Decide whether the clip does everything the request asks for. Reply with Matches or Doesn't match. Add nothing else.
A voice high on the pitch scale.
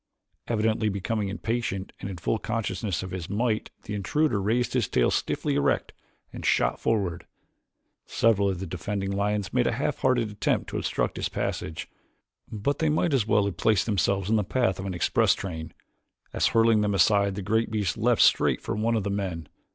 Doesn't match